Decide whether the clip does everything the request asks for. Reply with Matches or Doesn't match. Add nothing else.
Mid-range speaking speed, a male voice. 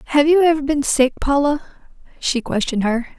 Doesn't match